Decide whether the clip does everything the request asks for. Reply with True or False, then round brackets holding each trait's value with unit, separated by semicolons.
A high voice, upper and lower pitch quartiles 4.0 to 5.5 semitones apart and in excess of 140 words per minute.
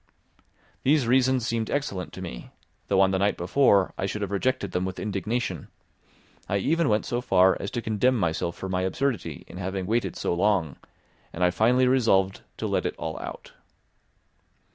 False (100 Hz; 4.8 semitones; 180 wpm)